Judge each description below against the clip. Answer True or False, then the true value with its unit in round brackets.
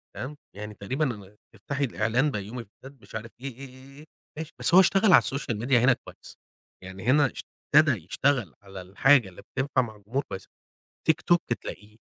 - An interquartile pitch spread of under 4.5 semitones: False (5.0 semitones)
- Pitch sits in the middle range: False (125 Hz)